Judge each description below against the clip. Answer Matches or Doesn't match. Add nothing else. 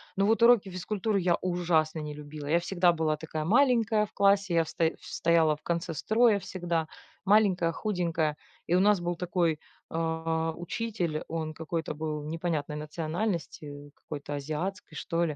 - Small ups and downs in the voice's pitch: Doesn't match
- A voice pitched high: Doesn't match